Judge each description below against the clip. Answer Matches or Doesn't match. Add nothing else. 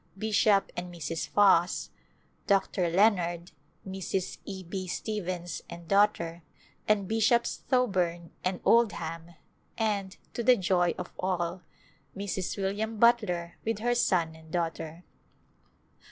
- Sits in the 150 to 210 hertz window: Matches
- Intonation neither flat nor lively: Matches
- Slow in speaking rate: Matches